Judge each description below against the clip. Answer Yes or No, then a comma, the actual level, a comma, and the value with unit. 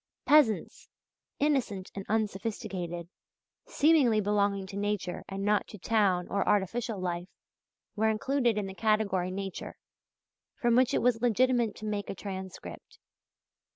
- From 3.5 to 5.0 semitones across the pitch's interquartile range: No, average, 3.1 semitones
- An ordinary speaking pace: No, slow, 130 wpm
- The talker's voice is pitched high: Yes, high, 210 Hz